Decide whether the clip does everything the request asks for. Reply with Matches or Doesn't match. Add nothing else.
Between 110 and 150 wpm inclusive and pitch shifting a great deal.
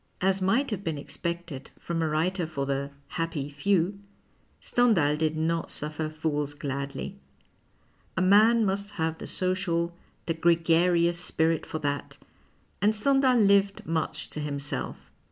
Doesn't match